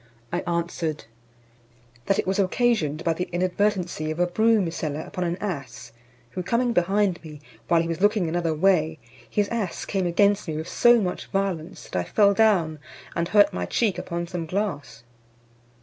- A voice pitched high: No, medium, 180 Hz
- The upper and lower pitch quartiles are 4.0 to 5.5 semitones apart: No, average, 3.6 semitones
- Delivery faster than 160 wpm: Yes, average, 175 wpm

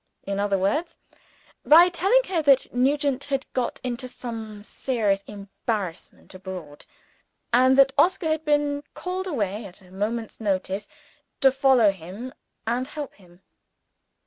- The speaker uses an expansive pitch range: Yes, wide, 6.2 semitones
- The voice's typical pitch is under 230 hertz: No, high, 240 Hz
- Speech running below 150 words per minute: Yes, slow, 135 wpm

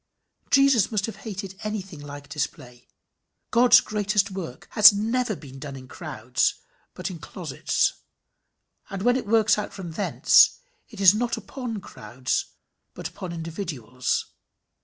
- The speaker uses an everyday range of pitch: No, wide, 6.7 semitones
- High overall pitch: Yes, high, 195 Hz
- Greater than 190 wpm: No, average, 140 wpm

